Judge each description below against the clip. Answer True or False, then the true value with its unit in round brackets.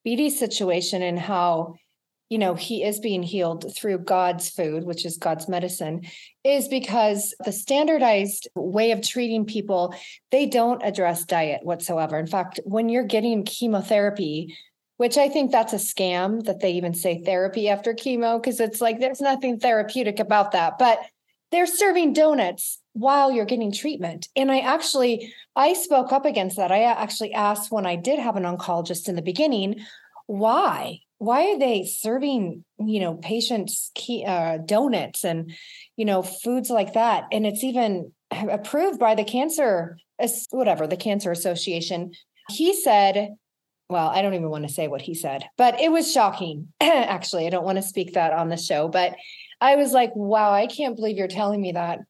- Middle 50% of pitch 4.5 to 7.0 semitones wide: True (5.2 semitones)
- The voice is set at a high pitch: True (210 Hz)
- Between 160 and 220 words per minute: True (175 wpm)